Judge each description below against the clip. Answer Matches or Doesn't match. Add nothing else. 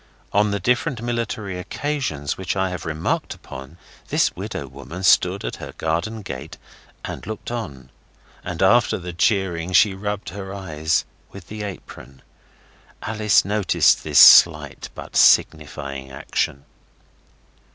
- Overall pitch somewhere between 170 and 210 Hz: Doesn't match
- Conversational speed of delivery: Doesn't match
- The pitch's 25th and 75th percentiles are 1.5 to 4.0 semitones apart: Doesn't match